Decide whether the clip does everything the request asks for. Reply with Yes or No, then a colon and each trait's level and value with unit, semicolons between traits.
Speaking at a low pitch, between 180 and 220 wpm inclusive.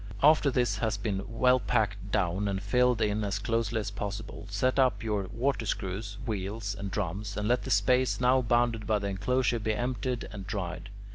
Yes: low, 110 Hz; average, 190 wpm